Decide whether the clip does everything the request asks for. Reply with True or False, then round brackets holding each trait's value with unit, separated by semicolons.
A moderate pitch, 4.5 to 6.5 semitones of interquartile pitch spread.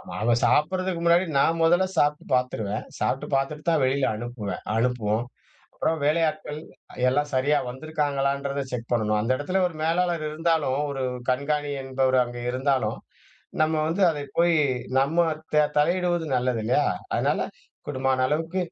False (145 Hz; 4.0 semitones)